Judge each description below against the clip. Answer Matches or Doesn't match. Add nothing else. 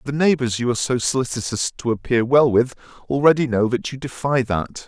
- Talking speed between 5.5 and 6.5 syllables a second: Matches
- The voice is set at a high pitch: Doesn't match